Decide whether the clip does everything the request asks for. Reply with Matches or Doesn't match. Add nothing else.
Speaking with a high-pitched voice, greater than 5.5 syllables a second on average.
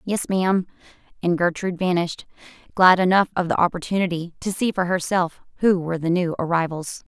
Doesn't match